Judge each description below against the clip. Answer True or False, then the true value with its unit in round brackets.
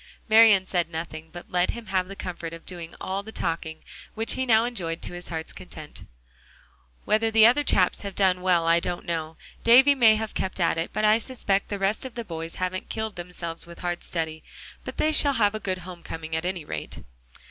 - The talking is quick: True (215 wpm)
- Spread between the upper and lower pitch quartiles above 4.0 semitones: True (4.6 semitones)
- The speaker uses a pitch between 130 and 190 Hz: True (185 Hz)